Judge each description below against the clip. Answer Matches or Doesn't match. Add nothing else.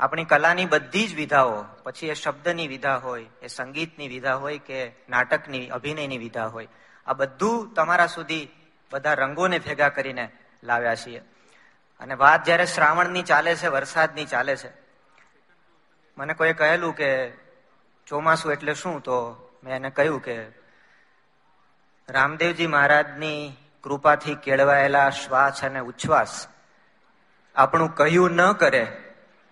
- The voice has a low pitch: Doesn't match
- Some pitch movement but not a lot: Matches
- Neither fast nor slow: Matches